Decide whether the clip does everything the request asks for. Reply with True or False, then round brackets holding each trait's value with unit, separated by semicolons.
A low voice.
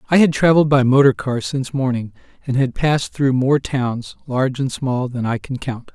True (130 Hz)